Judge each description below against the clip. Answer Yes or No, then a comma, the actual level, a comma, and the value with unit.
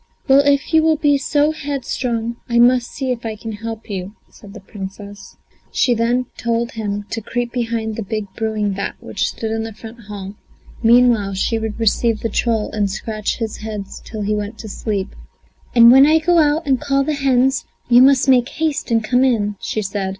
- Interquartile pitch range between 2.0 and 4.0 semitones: Yes, average, 3.3 semitones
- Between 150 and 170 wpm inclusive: No, average, 200 wpm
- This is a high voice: Yes, high, 230 Hz